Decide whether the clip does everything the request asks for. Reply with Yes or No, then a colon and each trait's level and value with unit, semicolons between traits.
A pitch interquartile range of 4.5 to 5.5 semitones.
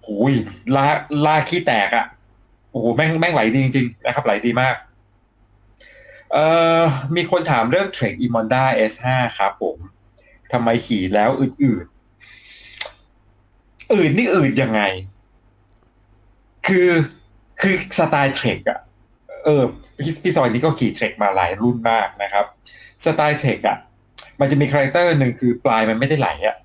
Yes: average, 5.2 semitones